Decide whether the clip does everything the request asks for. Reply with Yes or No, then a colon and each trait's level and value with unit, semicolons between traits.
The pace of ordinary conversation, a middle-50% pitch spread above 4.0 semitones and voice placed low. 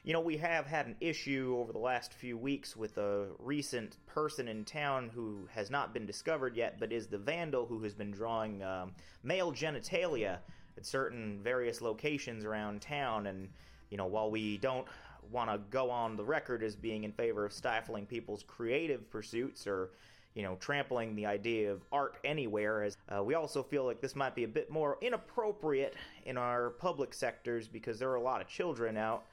Yes: average, 195 wpm; average, 4.5 semitones; low, 115 Hz